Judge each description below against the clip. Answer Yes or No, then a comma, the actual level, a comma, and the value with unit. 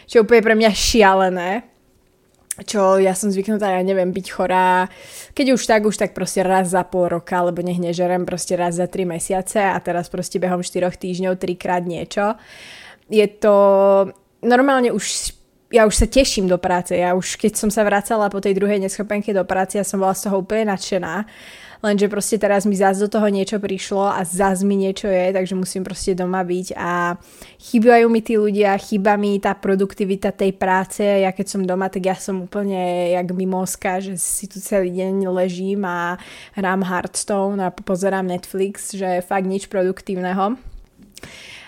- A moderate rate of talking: No, fast, 180 wpm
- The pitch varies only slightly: Yes, narrow, 1.9 semitones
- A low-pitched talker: No, high, 195 Hz